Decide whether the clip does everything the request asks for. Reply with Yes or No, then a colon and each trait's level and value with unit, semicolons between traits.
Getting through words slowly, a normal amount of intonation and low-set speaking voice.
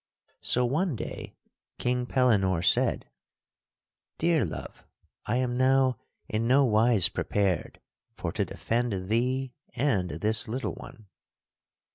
Yes: slow, 115 wpm; average, 3.2 semitones; low, 120 Hz